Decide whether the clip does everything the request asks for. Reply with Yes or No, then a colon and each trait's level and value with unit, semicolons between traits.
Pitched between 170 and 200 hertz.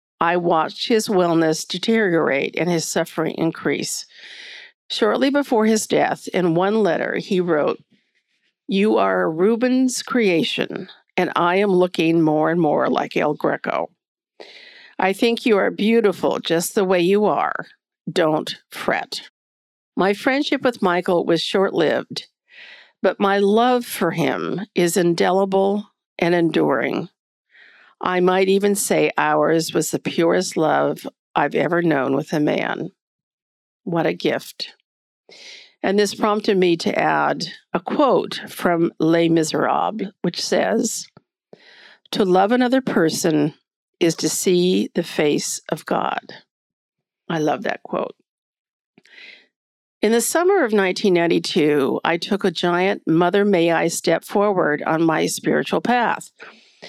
Yes: medium, 185 Hz